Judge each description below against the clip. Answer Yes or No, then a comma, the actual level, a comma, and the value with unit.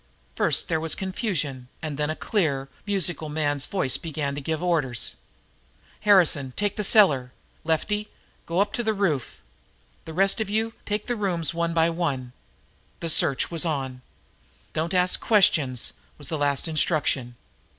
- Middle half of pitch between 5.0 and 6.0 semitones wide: Yes, average, 5.3 semitones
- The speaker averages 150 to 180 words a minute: Yes, average, 155 wpm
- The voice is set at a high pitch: No, medium, 160 Hz